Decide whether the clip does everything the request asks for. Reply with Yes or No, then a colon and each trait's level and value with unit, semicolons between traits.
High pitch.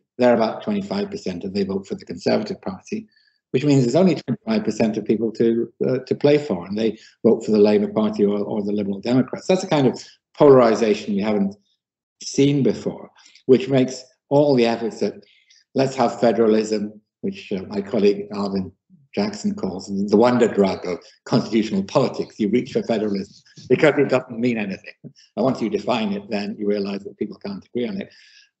No: low, 130 Hz